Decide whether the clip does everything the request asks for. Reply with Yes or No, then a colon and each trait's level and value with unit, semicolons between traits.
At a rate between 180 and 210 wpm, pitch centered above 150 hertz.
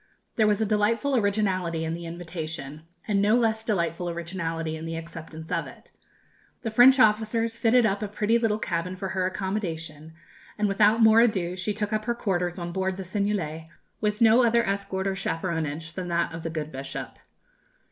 Yes: average, 190 wpm; high, 190 Hz